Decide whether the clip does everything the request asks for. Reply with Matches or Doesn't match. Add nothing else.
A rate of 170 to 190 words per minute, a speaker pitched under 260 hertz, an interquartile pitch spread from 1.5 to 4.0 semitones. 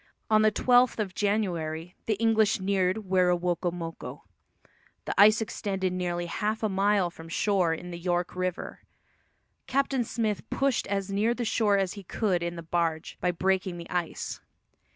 Doesn't match